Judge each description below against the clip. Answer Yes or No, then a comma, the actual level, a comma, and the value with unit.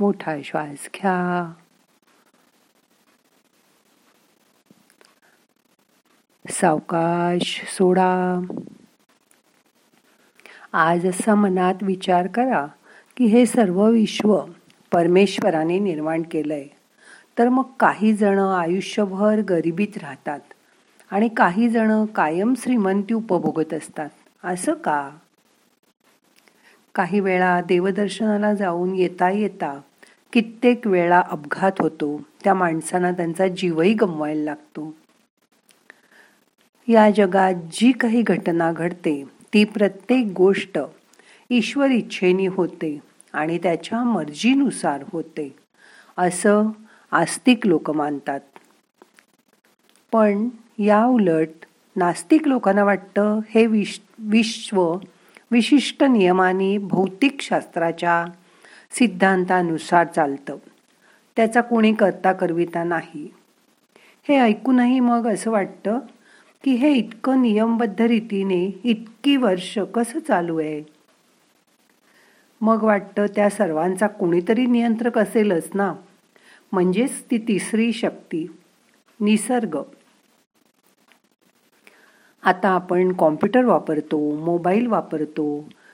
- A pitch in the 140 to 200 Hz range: Yes, high, 195 Hz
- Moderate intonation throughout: Yes, average, 4.5 semitones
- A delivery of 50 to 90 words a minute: Yes, average, 85 wpm